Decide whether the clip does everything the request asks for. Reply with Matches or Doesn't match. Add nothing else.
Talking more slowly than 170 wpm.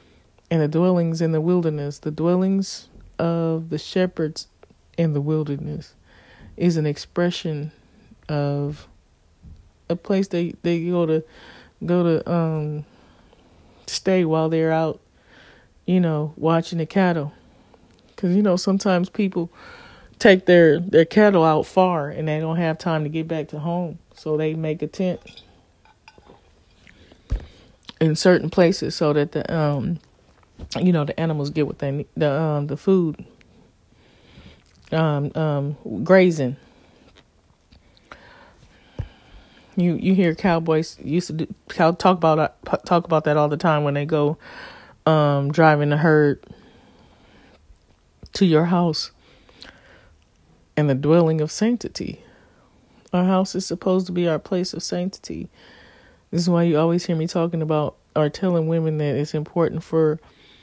Matches